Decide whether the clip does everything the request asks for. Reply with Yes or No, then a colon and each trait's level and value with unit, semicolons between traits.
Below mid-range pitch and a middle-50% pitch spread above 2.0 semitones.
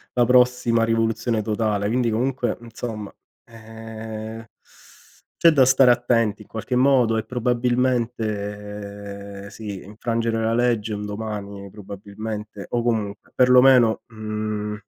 Yes: low, 110 Hz; narrow, 2.6 semitones